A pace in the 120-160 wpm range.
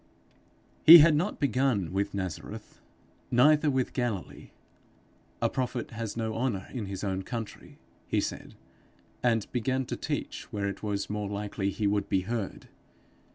Yes: average, 150 wpm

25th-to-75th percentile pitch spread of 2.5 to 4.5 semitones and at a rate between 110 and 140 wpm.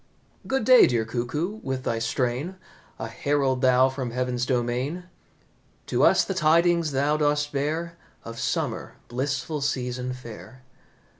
Yes: average, 3.6 semitones; slow, 135 wpm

